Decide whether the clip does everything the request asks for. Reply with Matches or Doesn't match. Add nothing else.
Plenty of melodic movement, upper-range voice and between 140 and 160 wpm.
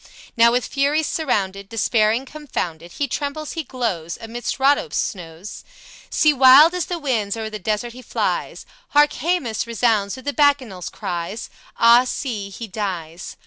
Matches